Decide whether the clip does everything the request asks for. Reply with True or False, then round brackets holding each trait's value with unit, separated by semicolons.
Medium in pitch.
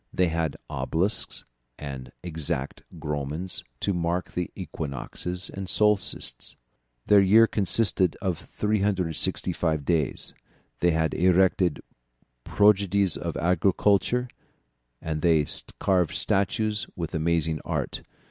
False (90 Hz)